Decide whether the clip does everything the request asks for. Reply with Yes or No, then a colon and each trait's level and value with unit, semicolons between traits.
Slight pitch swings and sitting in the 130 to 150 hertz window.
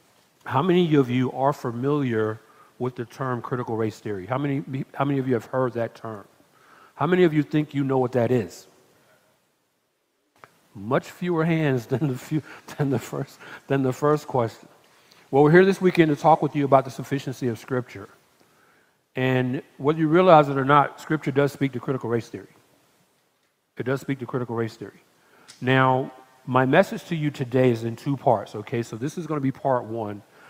No: average, 3.0 semitones; low, 135 Hz